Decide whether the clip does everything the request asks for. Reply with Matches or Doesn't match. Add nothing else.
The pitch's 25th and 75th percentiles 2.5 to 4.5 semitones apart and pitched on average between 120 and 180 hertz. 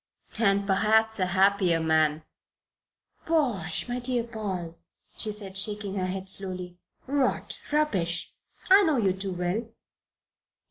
Doesn't match